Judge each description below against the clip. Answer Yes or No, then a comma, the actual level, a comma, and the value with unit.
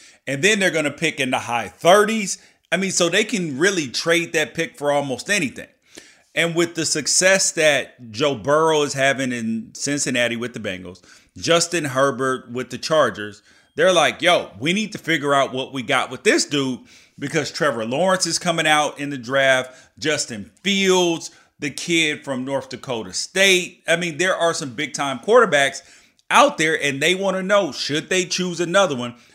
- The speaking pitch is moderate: Yes, medium, 150 Hz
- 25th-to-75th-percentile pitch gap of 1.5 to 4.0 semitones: No, average, 4.6 semitones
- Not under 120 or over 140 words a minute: No, average, 190 wpm